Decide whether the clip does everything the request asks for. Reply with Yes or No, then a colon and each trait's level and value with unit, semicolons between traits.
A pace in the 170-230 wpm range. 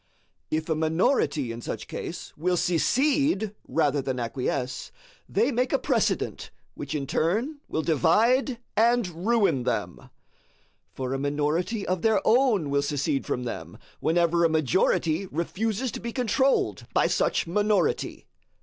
No: average, 140 wpm